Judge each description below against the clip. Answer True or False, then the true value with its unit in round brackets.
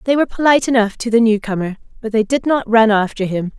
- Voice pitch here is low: False (225 Hz)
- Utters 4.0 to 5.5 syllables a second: False (6.5 syllables/s)